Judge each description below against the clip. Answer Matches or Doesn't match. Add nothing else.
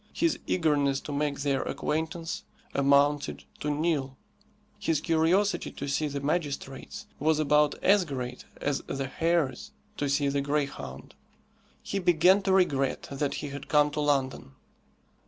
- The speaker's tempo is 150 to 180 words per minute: Doesn't match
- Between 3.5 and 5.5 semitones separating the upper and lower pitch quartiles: Doesn't match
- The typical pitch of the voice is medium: Matches